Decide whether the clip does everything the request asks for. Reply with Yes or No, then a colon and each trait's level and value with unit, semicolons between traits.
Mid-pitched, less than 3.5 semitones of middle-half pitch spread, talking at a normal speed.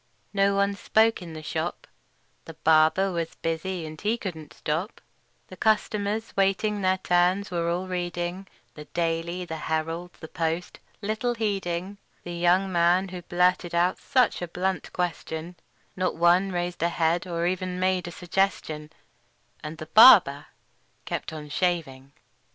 Yes: medium, 175 Hz; narrow, 2.6 semitones; average, 150 wpm